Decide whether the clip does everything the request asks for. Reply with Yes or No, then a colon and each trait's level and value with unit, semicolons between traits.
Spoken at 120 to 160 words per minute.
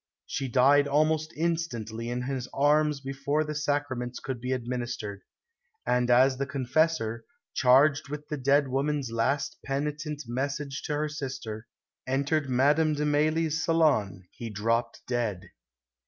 Yes: slow, 135 wpm